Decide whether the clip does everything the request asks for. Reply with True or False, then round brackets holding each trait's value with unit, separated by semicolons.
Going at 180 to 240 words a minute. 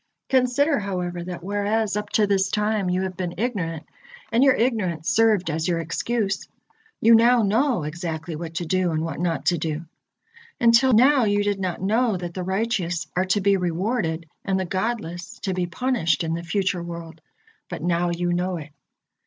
True (185 wpm)